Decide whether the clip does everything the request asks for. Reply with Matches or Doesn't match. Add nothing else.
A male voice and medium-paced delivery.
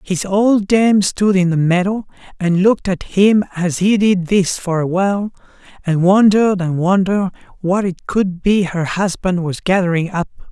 Matches